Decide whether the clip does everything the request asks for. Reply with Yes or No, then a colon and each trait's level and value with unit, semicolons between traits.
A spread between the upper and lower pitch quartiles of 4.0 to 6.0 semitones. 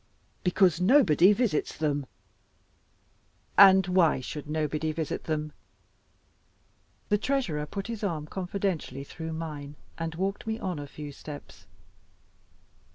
Yes: average, 4.3 semitones